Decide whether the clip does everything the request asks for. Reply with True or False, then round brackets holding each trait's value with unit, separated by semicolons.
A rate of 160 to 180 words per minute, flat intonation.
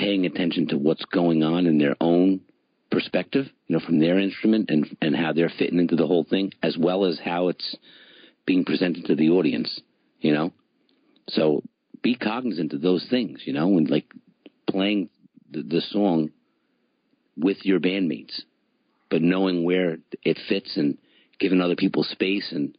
True (170 wpm; 2.3 semitones)